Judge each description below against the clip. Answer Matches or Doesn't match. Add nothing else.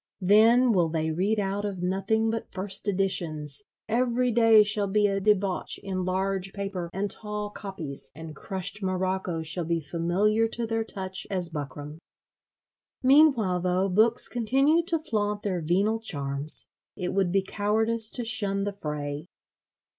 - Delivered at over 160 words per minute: Doesn't match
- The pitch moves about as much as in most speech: Matches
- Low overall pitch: Doesn't match